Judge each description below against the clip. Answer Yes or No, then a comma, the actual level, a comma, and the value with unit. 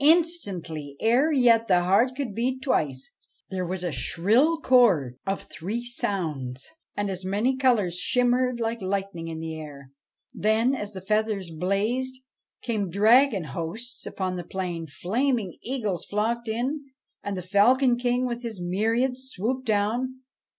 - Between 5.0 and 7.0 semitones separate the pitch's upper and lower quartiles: Yes, wide, 5.5 semitones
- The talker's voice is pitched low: No, high, 215 Hz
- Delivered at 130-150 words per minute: Yes, average, 145 wpm